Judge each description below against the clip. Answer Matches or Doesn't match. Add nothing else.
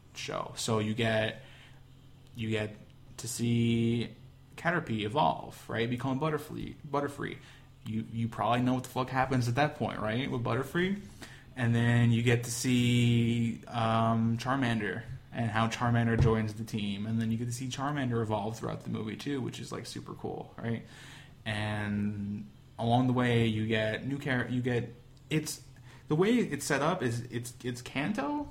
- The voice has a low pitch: Matches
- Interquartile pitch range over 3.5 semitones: Doesn't match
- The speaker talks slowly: Doesn't match